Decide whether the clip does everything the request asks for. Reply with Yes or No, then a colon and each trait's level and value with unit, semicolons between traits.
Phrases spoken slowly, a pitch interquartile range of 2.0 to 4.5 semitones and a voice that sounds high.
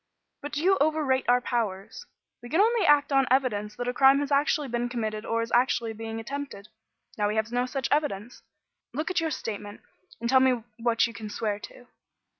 No: average, 200 wpm; average, 4.1 semitones; high, 245 Hz